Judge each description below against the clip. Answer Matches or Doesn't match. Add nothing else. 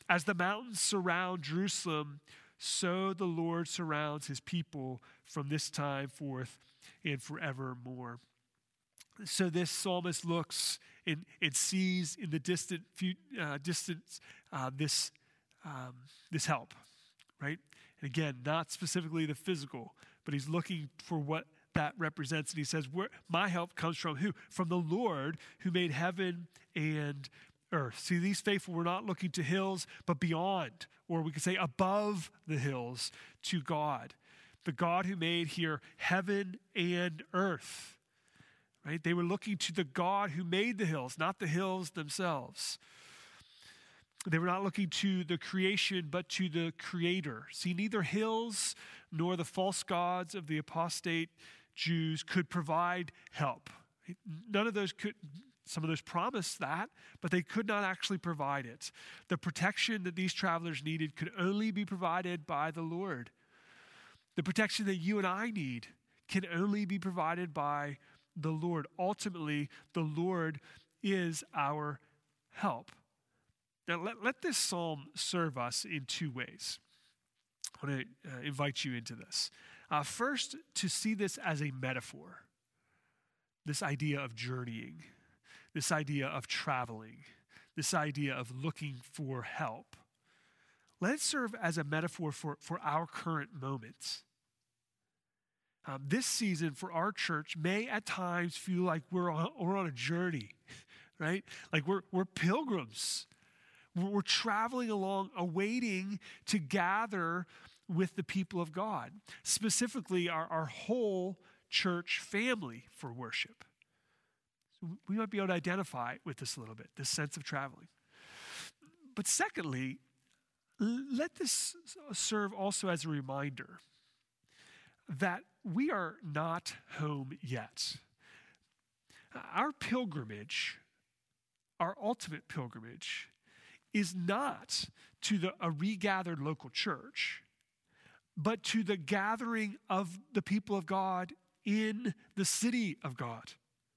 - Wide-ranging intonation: Doesn't match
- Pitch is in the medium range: Matches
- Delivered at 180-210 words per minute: Doesn't match